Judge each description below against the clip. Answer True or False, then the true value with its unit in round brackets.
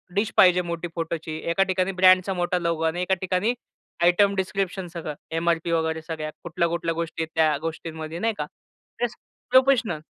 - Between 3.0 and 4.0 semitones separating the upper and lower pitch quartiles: False (2.6 semitones)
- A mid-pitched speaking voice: True (170 Hz)